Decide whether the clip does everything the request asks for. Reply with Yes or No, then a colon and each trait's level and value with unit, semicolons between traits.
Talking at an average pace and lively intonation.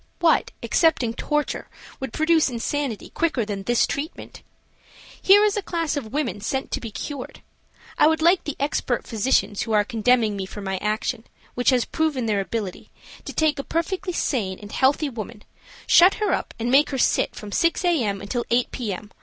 Yes: average, 190 wpm; wide, 6.5 semitones